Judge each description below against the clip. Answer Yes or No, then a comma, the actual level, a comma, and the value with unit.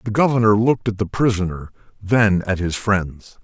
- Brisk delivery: No, average, 175 wpm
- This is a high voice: No, low, 105 Hz